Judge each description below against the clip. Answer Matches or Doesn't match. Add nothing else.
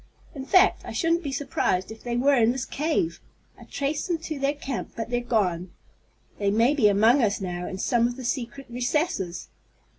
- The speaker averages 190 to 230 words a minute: Matches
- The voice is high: Matches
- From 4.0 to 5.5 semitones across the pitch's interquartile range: Matches